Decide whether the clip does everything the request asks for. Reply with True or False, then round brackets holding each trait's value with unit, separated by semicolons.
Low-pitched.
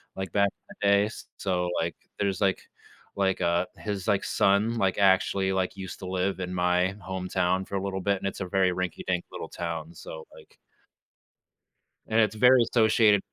True (95 Hz)